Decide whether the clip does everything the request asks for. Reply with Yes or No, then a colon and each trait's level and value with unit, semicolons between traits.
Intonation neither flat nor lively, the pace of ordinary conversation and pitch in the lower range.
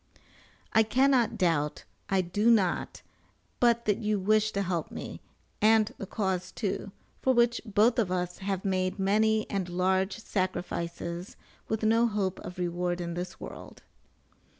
No: average, 3.2 semitones; average, 150 wpm; high, 195 Hz